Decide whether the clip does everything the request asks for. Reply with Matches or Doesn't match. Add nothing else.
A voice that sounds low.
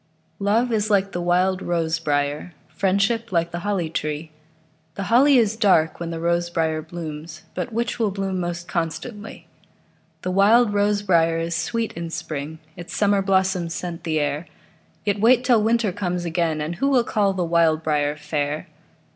Doesn't match